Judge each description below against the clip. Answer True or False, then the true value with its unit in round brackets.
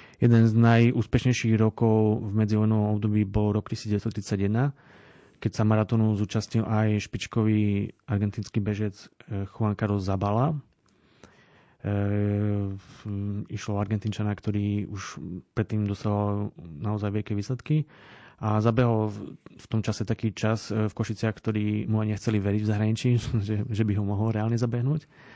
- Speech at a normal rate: True (130 wpm)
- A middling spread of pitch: False (1.6 semitones)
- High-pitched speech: False (110 Hz)